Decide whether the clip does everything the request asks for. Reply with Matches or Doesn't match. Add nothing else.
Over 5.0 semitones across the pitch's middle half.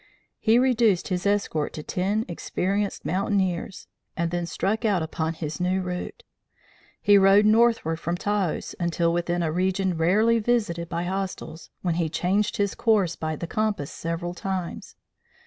Doesn't match